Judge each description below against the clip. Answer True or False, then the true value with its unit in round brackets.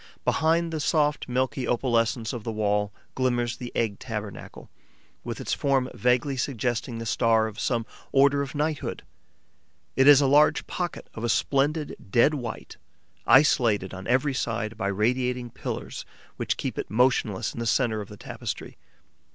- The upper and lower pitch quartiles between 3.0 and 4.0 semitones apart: True (3.5 semitones)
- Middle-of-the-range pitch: False (125 Hz)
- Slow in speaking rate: False (160 wpm)